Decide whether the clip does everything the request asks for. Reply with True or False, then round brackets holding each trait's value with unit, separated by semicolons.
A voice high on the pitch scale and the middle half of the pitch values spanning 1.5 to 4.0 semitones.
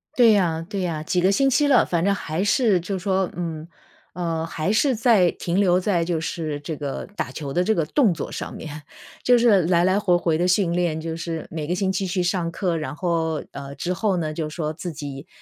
False (175 Hz; 3.3 semitones)